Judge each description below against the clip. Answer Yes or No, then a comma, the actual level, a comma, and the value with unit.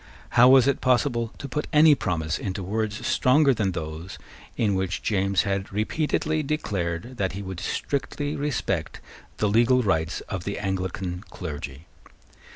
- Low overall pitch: Yes, low, 100 Hz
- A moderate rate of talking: Yes, average, 150 wpm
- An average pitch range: No, wide, 6.0 semitones